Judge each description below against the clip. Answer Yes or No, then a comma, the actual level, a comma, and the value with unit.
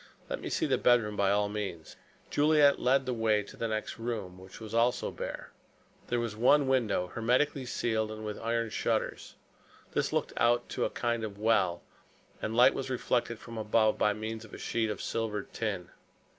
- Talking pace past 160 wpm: Yes, average, 195 wpm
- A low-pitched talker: Yes, low, 110 Hz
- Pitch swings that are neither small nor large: No, narrow, 2.3 semitones